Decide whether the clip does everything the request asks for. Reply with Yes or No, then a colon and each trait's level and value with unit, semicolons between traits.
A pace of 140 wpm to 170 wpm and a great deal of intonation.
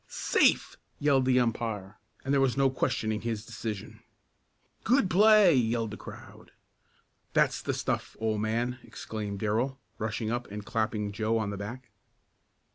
No: average, 145 wpm; average, 3.3 semitones